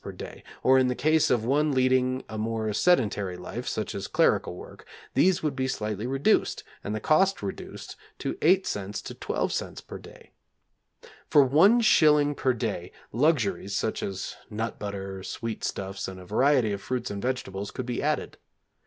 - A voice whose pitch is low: Yes, low, 120 Hz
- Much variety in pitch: Yes, wide, 5.9 semitones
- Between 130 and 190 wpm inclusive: Yes, average, 170 wpm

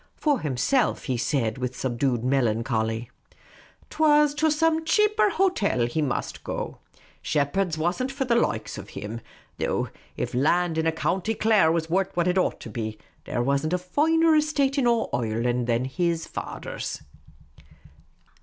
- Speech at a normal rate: Yes, average, 160 wpm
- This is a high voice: No, medium, 165 Hz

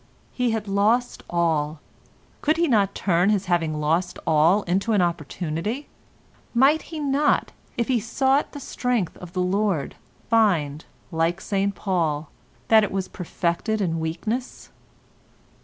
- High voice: Yes, high, 195 Hz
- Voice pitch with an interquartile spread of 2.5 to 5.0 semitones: No, wide, 5.4 semitones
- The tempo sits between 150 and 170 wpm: No, average, 140 wpm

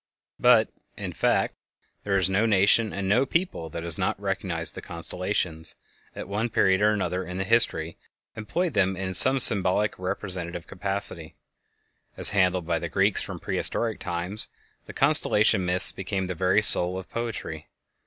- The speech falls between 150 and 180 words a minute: Yes, average, 165 wpm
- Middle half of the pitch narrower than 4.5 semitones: Yes, average, 2.8 semitones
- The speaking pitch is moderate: No, very low, 95 Hz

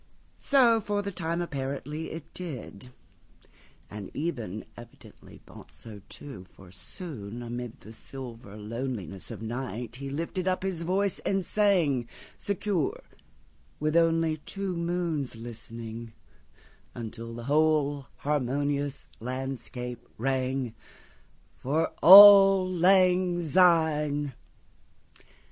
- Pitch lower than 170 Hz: Yes, medium, 140 Hz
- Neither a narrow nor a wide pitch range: No, wide, 6.6 semitones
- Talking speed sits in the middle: No, slow, 90 wpm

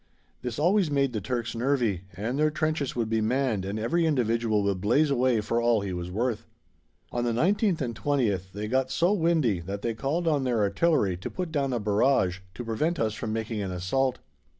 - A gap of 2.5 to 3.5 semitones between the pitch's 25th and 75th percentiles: No, average, 5.1 semitones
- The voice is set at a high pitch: No, low, 120 Hz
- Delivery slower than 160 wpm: No, fast, 205 wpm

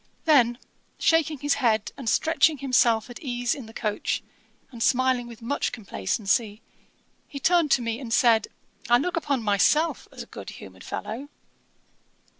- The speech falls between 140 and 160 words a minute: Yes, average, 155 wpm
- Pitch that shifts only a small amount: No, average, 4.1 semitones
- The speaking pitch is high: Yes, high, 245 Hz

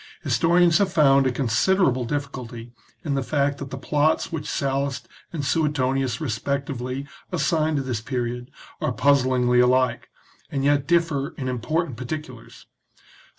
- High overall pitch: No, medium, 140 Hz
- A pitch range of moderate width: Yes, average, 3.0 semitones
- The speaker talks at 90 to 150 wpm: Yes, average, 140 wpm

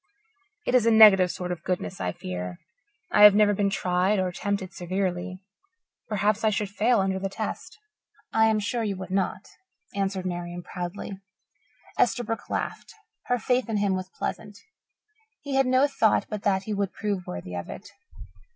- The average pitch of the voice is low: No, high, 200 Hz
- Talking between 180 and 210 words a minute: No, average, 170 wpm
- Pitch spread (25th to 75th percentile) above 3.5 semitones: No, narrow, 2.6 semitones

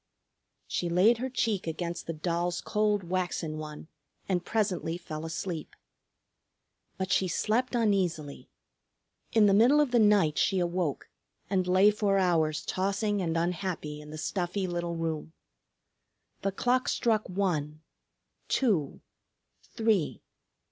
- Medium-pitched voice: Yes, medium, 180 Hz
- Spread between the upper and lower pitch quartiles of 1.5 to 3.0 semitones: No, average, 4.0 semitones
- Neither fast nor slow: No, slow, 125 wpm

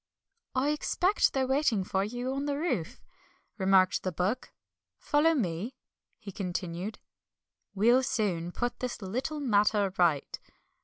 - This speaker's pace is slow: Yes, slow, 125 wpm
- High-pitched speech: Yes, high, 215 Hz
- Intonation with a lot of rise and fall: Yes, wide, 6.1 semitones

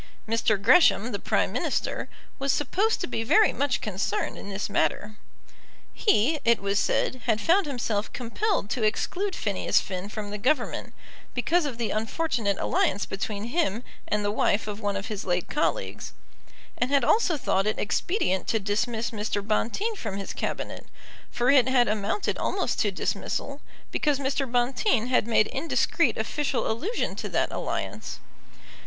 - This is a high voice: Yes, high, 230 Hz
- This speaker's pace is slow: No, average, 160 wpm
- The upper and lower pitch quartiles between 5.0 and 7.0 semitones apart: Yes, average, 5.3 semitones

